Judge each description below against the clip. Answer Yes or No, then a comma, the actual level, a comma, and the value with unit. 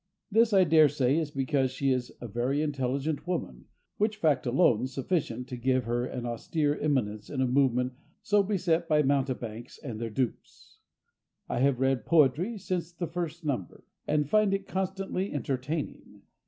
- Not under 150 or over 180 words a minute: Yes, average, 165 wpm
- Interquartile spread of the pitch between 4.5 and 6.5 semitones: Yes, average, 5.0 semitones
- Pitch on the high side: No, medium, 140 Hz